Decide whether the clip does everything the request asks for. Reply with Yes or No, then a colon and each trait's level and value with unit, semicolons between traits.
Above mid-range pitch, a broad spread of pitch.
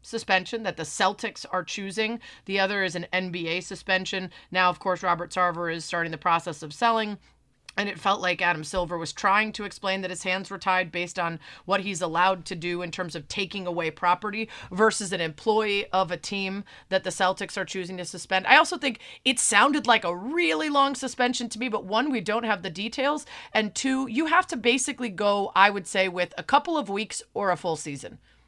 No: high, 195 Hz; average, 3.6 semitones